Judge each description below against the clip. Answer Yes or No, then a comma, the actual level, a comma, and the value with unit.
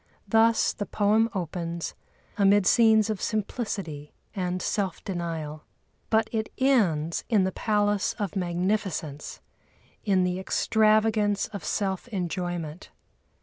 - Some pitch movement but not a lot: Yes, average, 3.7 semitones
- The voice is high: Yes, high, 195 Hz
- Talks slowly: Yes, slow, 110 wpm